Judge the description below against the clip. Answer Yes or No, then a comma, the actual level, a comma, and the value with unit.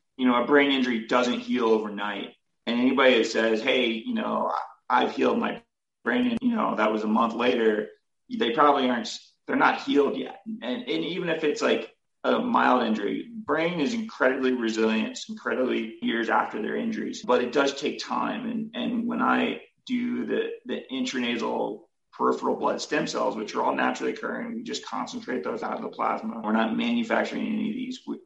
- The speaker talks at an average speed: Yes, average, 190 wpm